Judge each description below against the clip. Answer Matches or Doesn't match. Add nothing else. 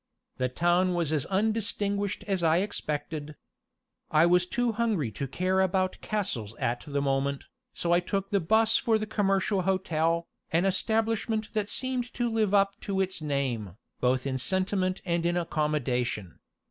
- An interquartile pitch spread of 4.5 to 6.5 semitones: Matches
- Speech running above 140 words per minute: Matches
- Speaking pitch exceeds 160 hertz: Matches